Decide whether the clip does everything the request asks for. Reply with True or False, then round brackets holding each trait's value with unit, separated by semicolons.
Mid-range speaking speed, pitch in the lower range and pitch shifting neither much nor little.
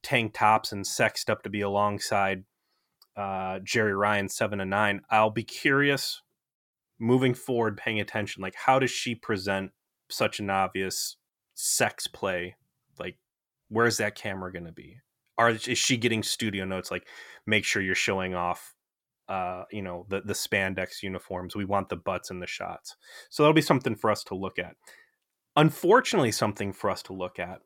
True (170 wpm; 105 Hz; 3.8 semitones)